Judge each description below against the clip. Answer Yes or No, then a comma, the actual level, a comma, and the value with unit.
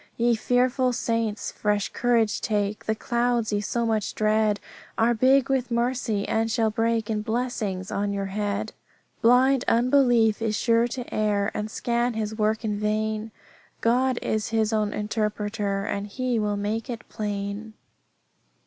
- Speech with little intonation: Yes, narrow, 2.2 semitones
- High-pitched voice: Yes, high, 220 Hz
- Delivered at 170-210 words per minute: No, average, 150 wpm